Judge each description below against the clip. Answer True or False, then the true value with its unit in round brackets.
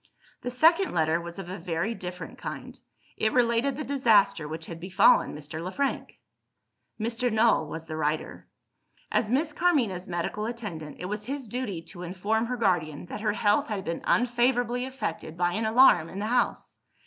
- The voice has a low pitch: False (210 Hz)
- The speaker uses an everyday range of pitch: False (6.0 semitones)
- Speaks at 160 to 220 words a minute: True (175 wpm)